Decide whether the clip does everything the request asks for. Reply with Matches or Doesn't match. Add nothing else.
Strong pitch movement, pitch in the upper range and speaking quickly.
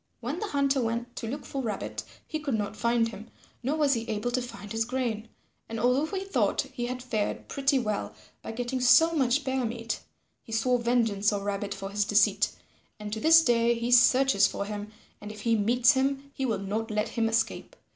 Doesn't match